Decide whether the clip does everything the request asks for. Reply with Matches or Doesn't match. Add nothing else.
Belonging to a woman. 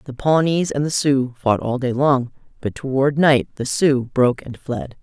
Matches